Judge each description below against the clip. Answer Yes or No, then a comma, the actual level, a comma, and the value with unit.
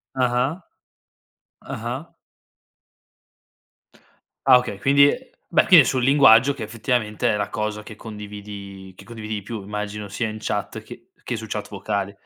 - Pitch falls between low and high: No, low, 110 Hz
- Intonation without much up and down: No, average, 3.3 semitones